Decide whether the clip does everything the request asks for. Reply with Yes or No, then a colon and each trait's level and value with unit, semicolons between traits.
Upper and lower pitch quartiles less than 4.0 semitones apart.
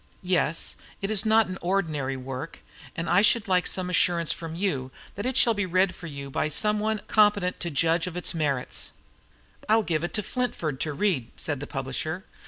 No: average, 5.2 semitones